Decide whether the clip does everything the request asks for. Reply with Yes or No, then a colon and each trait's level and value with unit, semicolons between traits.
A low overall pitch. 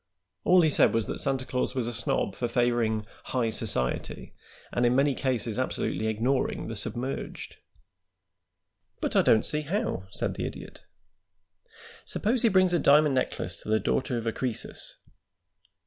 Yes: low, 125 Hz